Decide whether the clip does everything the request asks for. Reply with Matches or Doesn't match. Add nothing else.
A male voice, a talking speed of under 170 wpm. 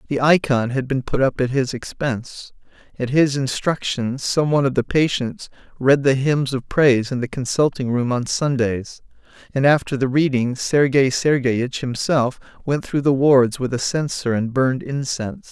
Doesn't match